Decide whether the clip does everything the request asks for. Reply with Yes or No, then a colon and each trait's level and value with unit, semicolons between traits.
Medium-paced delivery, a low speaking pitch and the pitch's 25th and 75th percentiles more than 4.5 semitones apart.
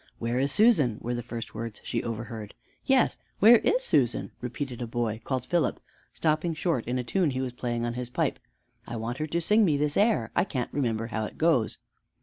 No: fast, 210 wpm; low, 125 Hz; average, 5.2 semitones